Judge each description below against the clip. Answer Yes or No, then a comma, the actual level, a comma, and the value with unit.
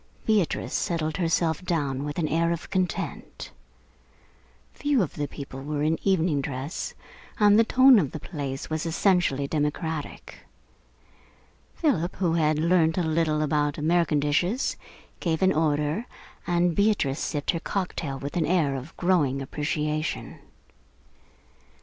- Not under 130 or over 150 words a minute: Yes, slow, 135 wpm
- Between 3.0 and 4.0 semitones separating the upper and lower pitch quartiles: Yes, average, 3.3 semitones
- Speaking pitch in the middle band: Yes, medium, 160 Hz